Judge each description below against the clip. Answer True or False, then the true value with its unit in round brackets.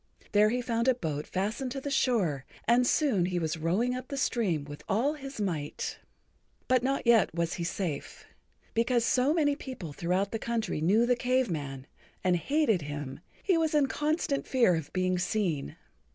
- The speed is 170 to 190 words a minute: True (185 wpm)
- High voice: True (220 Hz)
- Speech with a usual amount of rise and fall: False (7.2 semitones)